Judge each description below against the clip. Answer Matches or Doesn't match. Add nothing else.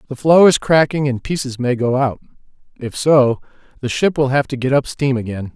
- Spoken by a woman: Doesn't match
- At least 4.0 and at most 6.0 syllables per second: Matches